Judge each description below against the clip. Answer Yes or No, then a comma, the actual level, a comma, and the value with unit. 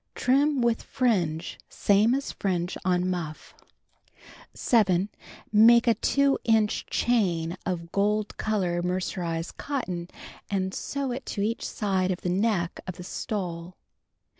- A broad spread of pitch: No, average, 4.4 semitones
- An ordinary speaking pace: No, slow, 130 wpm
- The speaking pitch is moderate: No, high, 195 Hz